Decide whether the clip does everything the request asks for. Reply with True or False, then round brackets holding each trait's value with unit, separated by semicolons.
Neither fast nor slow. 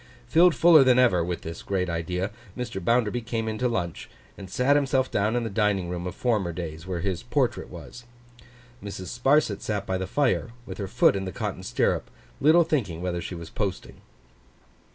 True (195 wpm)